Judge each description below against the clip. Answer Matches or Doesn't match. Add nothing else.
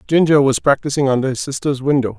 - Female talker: Doesn't match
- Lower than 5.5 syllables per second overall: Doesn't match